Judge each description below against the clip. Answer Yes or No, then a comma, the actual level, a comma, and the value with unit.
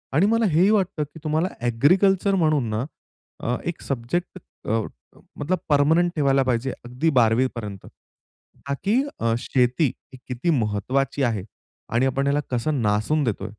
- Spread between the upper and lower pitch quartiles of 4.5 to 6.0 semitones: Yes, wide, 5.4 semitones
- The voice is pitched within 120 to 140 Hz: Yes, low, 135 Hz